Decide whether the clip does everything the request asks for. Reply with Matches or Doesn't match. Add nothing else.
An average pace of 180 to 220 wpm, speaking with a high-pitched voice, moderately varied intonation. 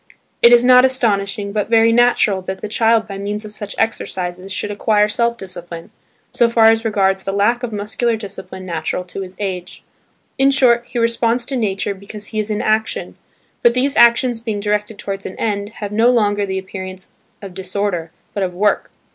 Matches